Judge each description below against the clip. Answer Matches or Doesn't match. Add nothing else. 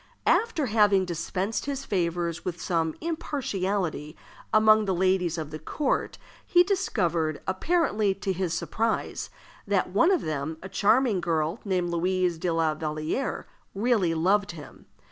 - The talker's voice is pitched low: Doesn't match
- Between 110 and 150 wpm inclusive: Matches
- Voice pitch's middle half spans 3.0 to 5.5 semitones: Matches